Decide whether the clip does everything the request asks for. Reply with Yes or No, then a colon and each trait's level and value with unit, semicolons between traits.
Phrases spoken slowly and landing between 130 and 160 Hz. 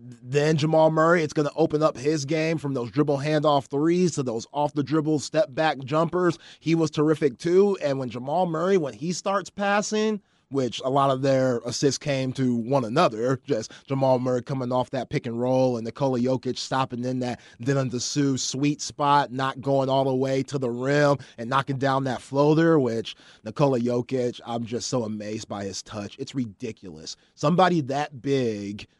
No: average, 190 wpm; low, 135 Hz